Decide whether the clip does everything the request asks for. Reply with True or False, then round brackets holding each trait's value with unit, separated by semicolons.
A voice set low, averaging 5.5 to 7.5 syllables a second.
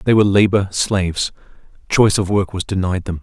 True (95 Hz; 6.0 syllables/s)